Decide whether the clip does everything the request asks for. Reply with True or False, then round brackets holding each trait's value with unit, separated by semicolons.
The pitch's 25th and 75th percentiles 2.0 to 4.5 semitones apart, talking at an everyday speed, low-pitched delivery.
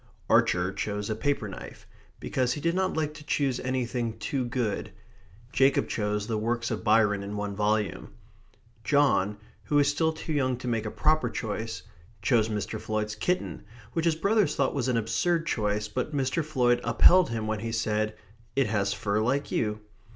False (5.1 semitones; 175 wpm; 115 Hz)